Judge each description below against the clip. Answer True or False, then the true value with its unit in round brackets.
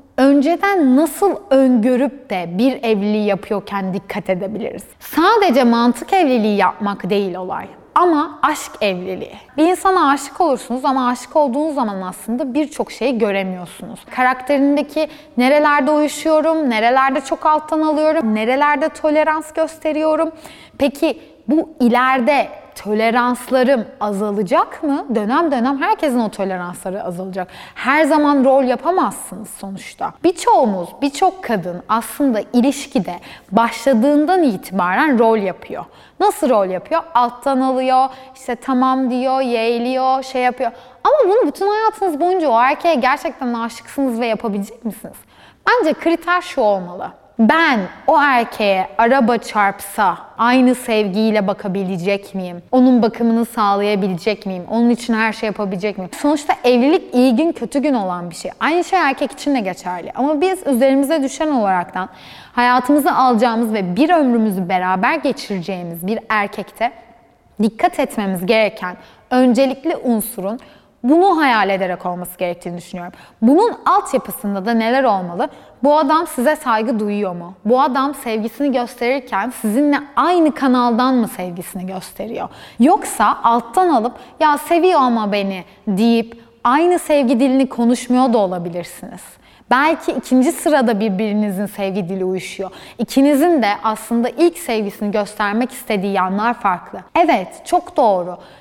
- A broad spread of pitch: True (5.9 semitones)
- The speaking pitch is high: True (245 Hz)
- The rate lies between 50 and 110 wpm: False (125 wpm)